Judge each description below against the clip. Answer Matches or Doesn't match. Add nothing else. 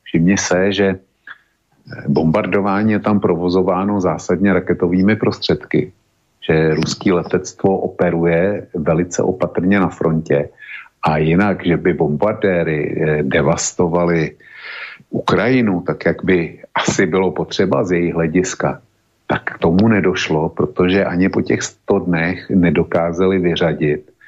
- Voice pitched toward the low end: Matches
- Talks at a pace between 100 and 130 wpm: Matches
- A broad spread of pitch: Doesn't match